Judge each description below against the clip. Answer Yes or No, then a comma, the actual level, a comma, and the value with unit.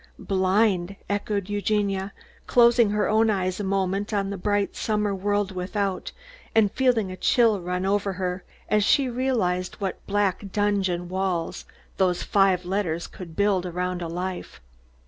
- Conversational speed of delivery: Yes, average, 145 wpm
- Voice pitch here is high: Yes, high, 195 Hz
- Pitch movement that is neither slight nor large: No, narrow, 2.1 semitones